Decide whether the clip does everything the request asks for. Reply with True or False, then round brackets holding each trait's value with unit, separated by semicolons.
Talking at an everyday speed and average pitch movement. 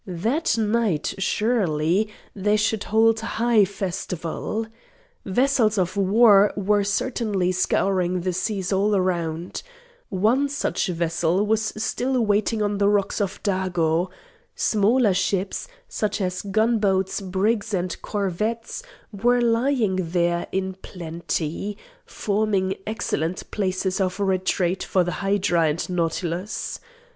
False (115 wpm; 3.0 semitones)